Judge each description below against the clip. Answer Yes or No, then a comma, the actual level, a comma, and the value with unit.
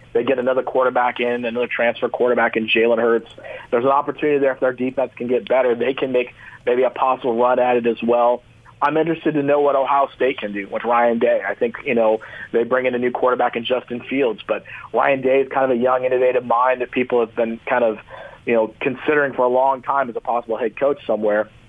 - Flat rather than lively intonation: Yes, narrow, 2.1 semitones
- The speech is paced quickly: Yes, fast, 240 wpm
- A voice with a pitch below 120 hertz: No, low, 125 Hz